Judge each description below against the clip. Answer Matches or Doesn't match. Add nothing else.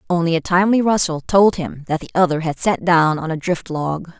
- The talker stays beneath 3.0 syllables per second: Doesn't match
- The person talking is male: Doesn't match